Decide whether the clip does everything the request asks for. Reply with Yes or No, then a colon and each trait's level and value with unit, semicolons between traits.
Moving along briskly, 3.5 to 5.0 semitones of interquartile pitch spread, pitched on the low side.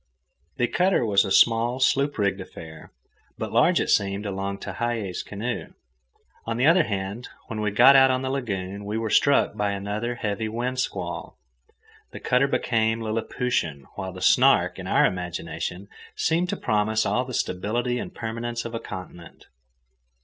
No: average, 165 wpm; average, 3.8 semitones; low, 110 Hz